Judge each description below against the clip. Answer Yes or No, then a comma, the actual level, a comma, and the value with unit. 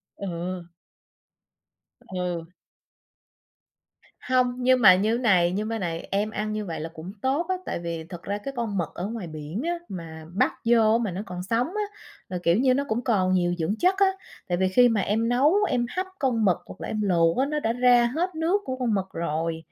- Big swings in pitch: Yes, wide, 5.9 semitones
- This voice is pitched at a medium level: No, high, 210 Hz